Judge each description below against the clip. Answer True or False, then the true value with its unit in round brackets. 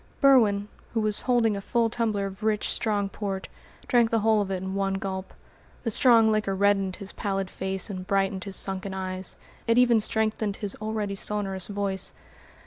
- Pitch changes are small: True (2.2 semitones)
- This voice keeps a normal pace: True (180 wpm)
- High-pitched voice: True (200 Hz)